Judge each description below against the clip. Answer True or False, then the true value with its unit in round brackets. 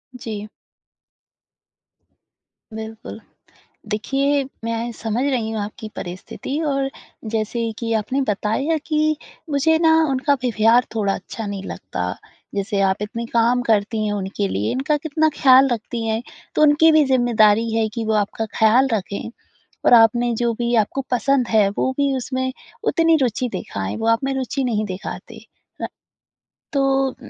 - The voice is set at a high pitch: True (230 Hz)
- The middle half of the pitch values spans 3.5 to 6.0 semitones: True (3.9 semitones)